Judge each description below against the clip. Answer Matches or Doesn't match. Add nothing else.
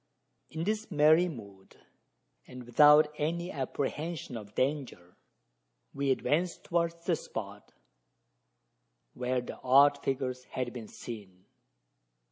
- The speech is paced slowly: Matches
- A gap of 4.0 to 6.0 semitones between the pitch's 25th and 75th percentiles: Matches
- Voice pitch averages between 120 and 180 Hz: Matches